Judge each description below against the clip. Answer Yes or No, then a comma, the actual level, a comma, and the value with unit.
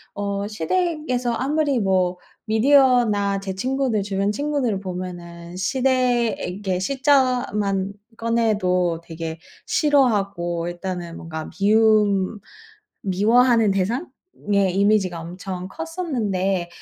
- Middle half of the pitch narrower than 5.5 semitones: Yes, average, 5.1 semitones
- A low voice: No, high, 205 Hz